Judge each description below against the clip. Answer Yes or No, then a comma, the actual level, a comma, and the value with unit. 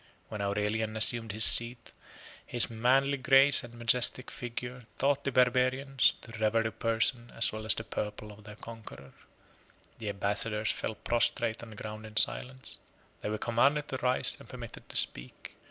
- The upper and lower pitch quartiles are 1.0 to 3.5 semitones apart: Yes, average, 2.8 semitones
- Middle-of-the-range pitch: No, low, 115 Hz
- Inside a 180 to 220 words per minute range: No, average, 170 wpm